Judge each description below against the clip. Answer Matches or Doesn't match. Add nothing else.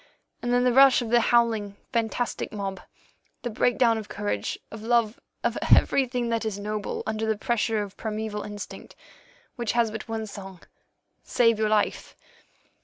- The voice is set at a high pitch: Matches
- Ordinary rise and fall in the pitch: Doesn't match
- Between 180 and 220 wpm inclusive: Doesn't match